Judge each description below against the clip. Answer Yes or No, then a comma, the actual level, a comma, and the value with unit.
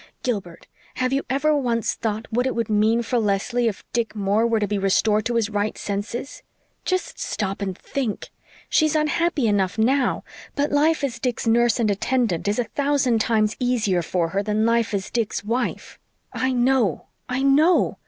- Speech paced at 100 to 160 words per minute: No, average, 180 wpm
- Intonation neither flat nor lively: Yes, average, 3.8 semitones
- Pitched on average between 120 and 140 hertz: No, high, 230 Hz